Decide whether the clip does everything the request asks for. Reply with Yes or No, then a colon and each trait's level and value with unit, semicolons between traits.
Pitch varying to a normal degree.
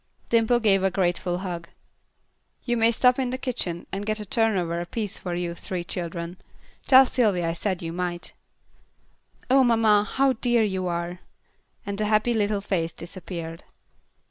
Yes: average, 4.6 semitones